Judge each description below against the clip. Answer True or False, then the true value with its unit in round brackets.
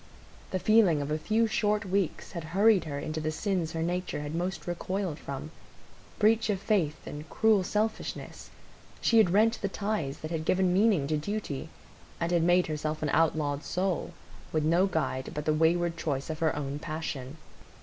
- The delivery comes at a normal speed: True (180 wpm)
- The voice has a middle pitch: True (170 Hz)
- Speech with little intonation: False (4.3 semitones)